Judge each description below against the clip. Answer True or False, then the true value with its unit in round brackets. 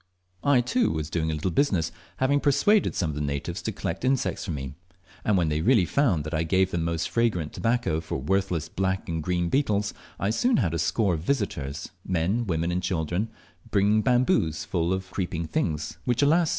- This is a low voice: True (90 Hz)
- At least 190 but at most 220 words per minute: True (195 wpm)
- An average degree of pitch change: False (6.3 semitones)